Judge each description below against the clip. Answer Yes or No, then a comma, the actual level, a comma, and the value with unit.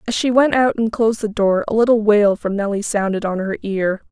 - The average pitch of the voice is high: Yes, high, 210 Hz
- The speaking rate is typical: No, fast, 250 wpm